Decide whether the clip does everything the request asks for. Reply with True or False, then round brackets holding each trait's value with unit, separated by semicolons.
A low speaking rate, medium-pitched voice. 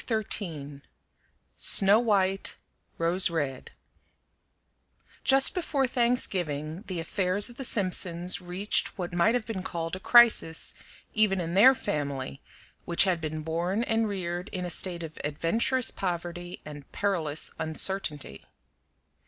True (125 wpm; 180 Hz)